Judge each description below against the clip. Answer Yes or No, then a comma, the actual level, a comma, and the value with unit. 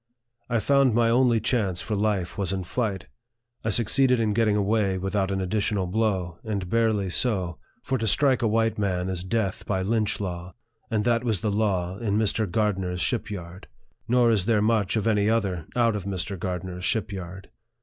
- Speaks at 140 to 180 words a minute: No, average, 190 wpm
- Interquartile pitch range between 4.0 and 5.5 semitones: No, average, 3.3 semitones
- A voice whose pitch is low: Yes, low, 105 Hz